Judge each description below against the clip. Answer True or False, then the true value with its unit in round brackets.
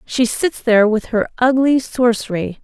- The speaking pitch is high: True (235 Hz)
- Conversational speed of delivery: True (160 wpm)